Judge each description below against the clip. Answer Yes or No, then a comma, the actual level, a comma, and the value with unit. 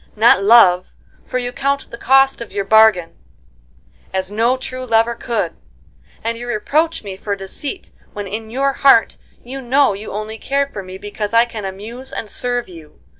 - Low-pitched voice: No, high, 230 Hz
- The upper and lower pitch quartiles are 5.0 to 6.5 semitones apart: No, average, 3.9 semitones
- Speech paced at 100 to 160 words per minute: No, average, 175 wpm